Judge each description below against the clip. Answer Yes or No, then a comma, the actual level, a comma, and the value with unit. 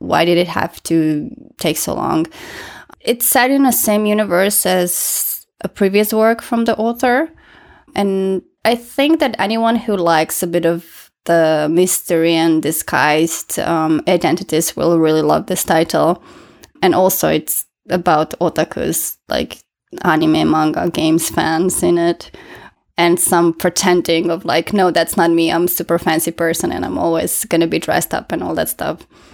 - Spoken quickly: No, average, 165 wpm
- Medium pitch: Yes, medium, 175 Hz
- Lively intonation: No, average, 4.0 semitones